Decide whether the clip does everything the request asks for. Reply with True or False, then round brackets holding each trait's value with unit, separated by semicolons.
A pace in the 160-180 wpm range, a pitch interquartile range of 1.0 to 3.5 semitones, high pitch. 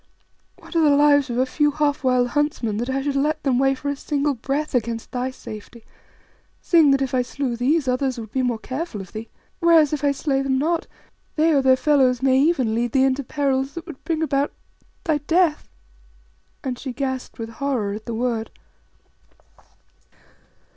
False (190 wpm; 2.9 semitones; 270 Hz)